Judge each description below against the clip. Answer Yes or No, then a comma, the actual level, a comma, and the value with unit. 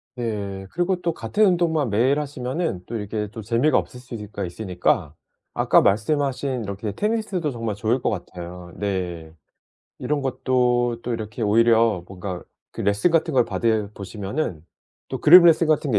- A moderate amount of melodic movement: No, wide, 6.1 semitones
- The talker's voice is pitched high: No, low, 115 Hz